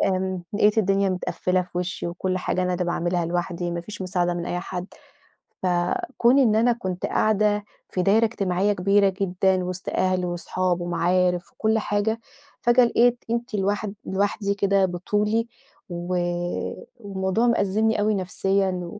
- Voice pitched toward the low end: No, high, 190 Hz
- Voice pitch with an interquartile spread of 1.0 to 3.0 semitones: Yes, narrow, 2.6 semitones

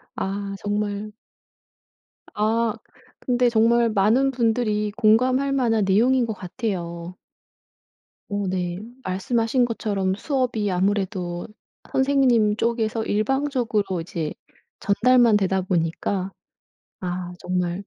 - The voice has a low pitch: No, high, 210 Hz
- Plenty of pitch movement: No, average, 3.9 semitones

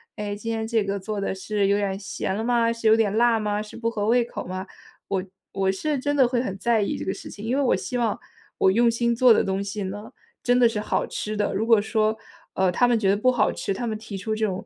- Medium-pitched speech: No, high, 215 Hz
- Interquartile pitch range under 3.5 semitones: Yes, average, 2.8 semitones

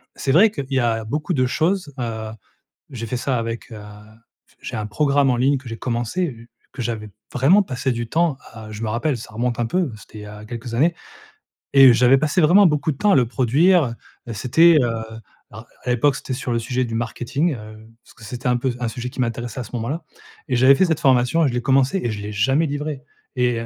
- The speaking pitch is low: Yes, low, 125 Hz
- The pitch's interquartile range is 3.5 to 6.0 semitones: Yes, average, 3.8 semitones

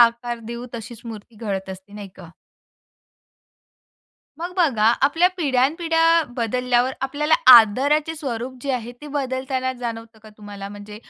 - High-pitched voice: Yes, high, 245 Hz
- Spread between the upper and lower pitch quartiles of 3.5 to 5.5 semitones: Yes, average, 4.4 semitones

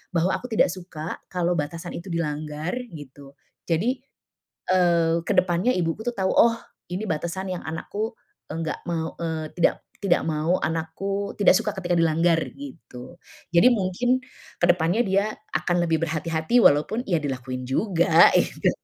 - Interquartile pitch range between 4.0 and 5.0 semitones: No, average, 3.1 semitones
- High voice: No, medium, 170 Hz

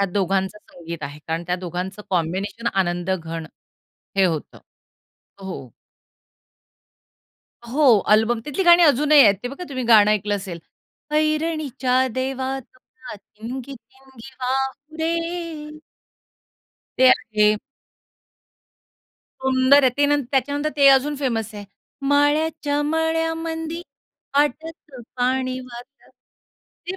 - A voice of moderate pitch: No, very high, 260 Hz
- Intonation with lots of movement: Yes, wide, 6.1 semitones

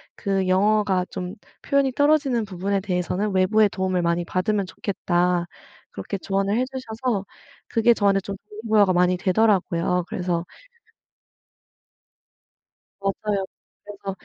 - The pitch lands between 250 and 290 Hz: No, high, 195 Hz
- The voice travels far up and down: No, average, 2.9 semitones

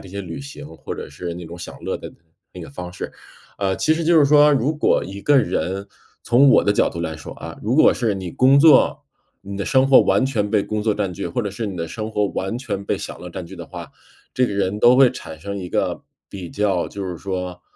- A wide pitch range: Yes, wide, 5.8 semitones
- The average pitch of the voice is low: Yes, low, 100 Hz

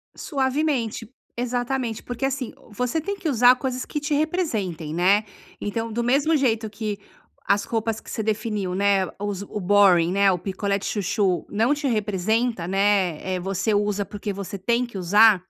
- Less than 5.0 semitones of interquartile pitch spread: Yes, average, 3.9 semitones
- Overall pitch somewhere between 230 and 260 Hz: No, high, 215 Hz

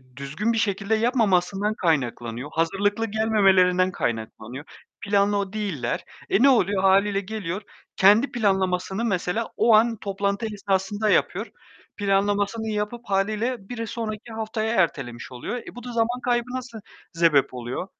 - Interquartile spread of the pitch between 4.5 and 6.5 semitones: No, average, 3.3 semitones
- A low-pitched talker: No, high, 200 Hz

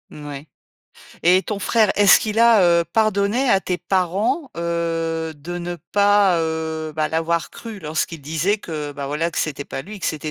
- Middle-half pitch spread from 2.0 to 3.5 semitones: No, average, 4.1 semitones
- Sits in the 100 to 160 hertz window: No, medium, 170 Hz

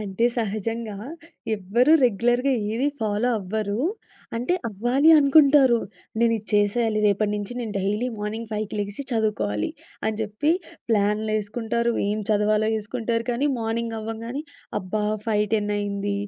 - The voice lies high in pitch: Yes, high, 220 Hz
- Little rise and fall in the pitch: Yes, narrow, 2.3 semitones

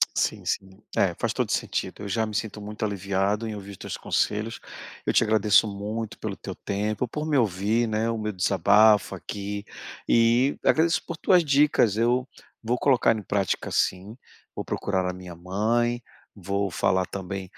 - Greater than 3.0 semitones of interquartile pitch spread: No, average, 2.7 semitones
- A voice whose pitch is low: Yes, low, 105 Hz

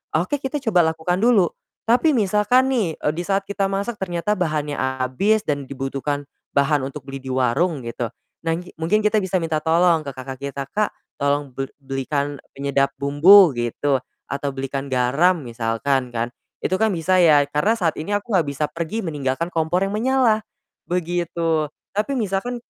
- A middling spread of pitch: No, wide, 5.9 semitones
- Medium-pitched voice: Yes, medium, 160 Hz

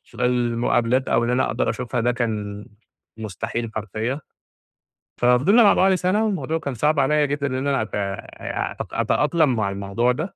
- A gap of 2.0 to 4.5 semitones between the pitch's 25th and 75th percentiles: No, average, 4.9 semitones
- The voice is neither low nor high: No, low, 125 Hz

